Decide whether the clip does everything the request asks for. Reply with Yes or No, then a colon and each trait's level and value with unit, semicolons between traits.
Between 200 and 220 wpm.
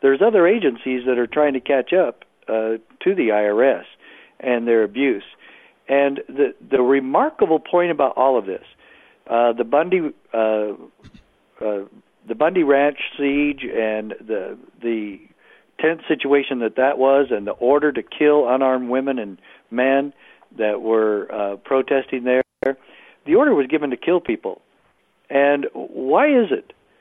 No: average, 150 wpm